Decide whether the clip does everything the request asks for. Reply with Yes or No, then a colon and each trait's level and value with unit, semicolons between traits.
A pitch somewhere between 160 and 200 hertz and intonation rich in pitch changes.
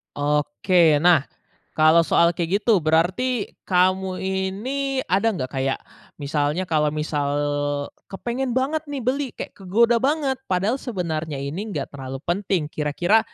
Yes: medium, 185 Hz; wide, 6.9 semitones